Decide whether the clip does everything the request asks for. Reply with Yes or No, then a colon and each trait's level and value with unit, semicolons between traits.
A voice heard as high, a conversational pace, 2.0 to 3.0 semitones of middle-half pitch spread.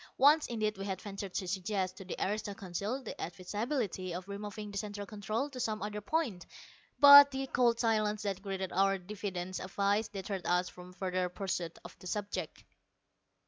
Yes: high, 200 Hz; average, 175 wpm; narrow, 2.5 semitones